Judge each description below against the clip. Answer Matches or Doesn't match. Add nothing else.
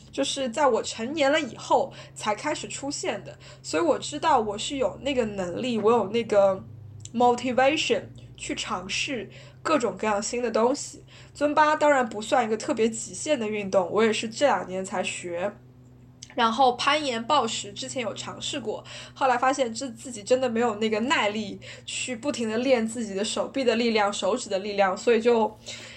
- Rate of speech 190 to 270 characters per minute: Doesn't match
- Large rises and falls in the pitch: Doesn't match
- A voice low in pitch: Doesn't match